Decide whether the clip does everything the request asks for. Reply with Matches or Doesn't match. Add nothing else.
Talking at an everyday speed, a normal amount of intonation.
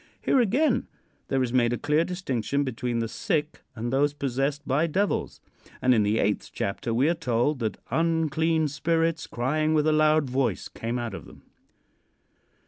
Matches